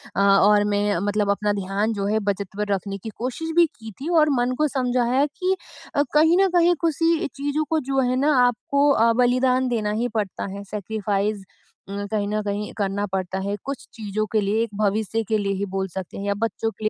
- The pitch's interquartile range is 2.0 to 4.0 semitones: No, average, 4.5 semitones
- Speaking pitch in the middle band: No, high, 220 Hz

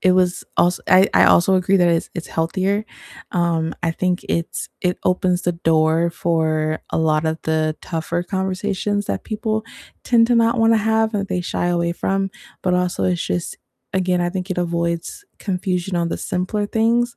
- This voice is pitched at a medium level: Yes, medium, 180 Hz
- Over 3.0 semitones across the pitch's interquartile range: No, average, 2.7 semitones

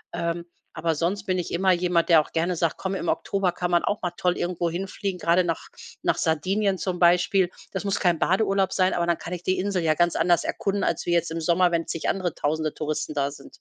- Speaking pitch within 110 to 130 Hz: No, medium, 175 Hz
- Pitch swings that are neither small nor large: No, narrow, 2.0 semitones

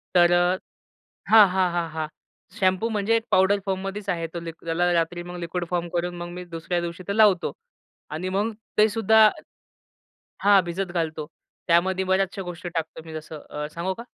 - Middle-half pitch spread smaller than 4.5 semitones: Yes, narrow, 2.4 semitones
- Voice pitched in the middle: Yes, medium, 180 Hz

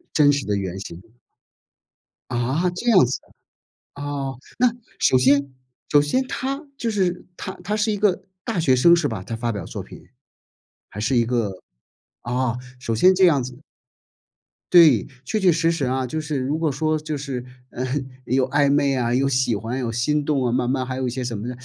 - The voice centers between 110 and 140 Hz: Yes, low, 135 Hz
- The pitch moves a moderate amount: Yes, average, 4.5 semitones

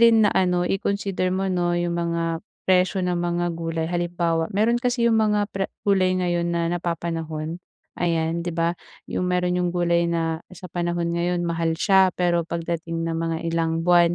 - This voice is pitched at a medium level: Yes, medium, 175 Hz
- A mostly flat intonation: Yes, narrow, 1.5 semitones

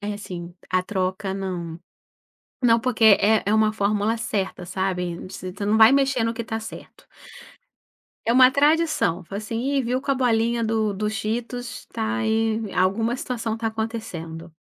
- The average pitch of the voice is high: Yes, high, 220 Hz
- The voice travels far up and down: No, average, 3.2 semitones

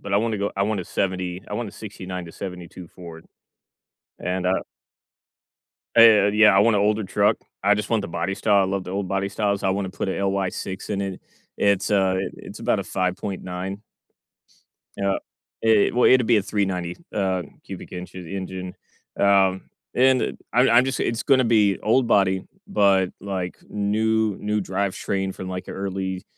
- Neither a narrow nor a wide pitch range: No, narrow, 2.1 semitones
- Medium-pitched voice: No, low, 100 Hz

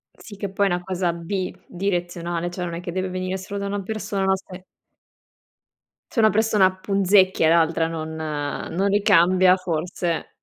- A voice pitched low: No, medium, 185 Hz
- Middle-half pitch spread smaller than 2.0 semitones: No, narrow, 2.4 semitones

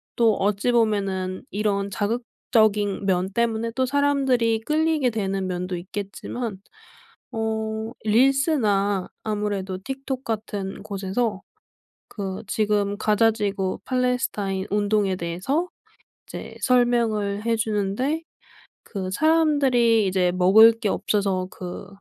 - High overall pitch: Yes, high, 215 Hz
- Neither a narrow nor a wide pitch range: Yes, average, 3.5 semitones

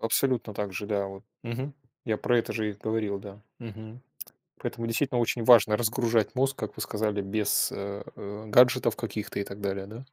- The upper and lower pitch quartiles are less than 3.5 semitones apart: Yes, average, 2.7 semitones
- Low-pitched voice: Yes, low, 110 Hz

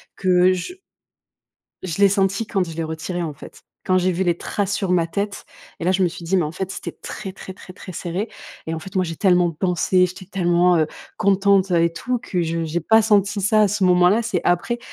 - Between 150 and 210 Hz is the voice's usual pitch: Yes, medium, 185 Hz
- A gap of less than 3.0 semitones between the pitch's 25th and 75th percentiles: Yes, narrow, 2.4 semitones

